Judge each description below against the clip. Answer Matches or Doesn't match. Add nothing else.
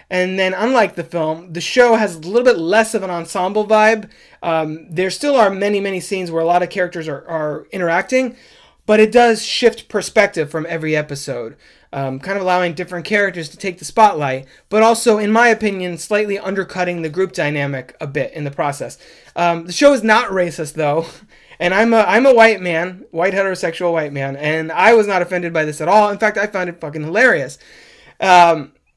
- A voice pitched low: Doesn't match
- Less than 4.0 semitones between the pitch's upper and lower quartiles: Doesn't match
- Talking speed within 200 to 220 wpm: Matches